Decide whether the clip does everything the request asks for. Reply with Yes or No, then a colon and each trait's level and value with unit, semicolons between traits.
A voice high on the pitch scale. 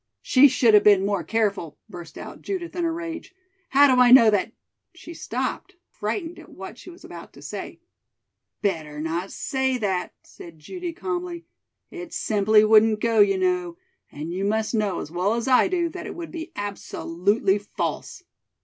Yes: high, 220 Hz